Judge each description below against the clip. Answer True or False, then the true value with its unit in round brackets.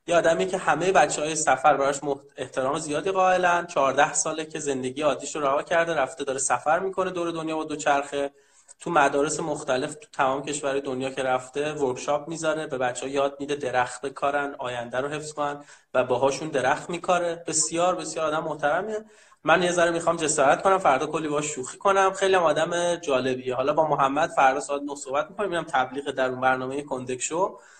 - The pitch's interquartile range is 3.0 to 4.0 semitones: True (3.3 semitones)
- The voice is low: False (150 Hz)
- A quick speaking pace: True (175 wpm)